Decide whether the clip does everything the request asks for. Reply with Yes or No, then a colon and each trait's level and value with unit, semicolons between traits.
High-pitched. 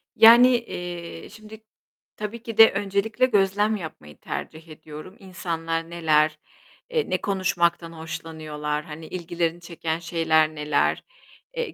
No: medium, 170 Hz